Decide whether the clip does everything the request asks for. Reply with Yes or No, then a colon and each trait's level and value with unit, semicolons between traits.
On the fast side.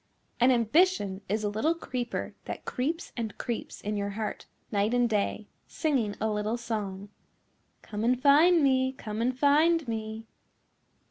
No: average, 150 wpm